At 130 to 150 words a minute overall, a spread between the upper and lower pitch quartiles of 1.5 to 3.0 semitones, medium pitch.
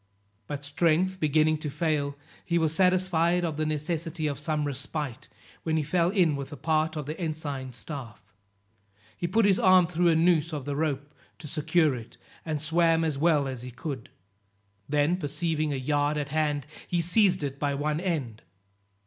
No: average, 175 wpm; narrow, 2.6 semitones; medium, 155 Hz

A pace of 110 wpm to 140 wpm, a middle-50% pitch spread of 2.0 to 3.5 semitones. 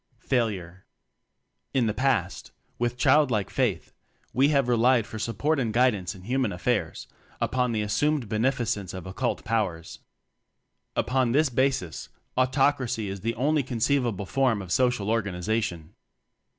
No: slow, 135 wpm; average, 4.2 semitones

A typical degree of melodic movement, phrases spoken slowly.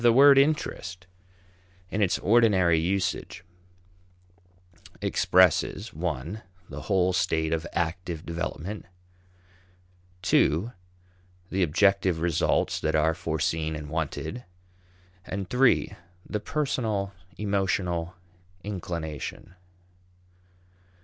Yes: average, 4.0 semitones; slow, 85 wpm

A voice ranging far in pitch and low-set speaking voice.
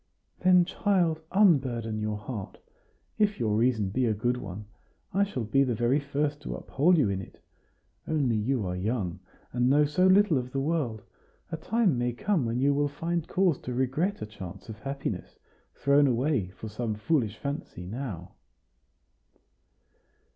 Yes: wide, 6.1 semitones; low, 130 Hz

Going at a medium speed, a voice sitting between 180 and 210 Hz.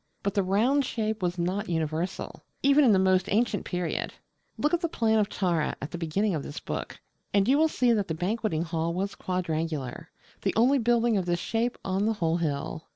No: fast, 210 wpm; high, 190 Hz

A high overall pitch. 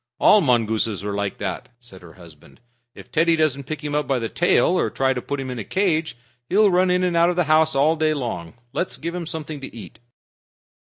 No: medium, 145 Hz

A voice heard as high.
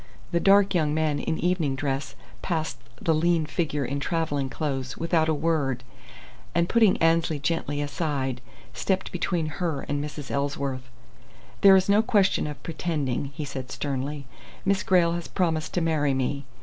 No: medium, 155 Hz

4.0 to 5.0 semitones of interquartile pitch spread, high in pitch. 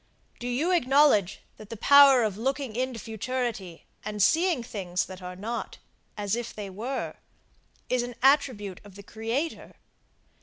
Yes: average, 4.4 semitones; high, 230 Hz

